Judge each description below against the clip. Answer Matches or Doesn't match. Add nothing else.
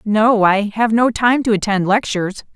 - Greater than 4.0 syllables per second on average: Matches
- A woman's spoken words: Matches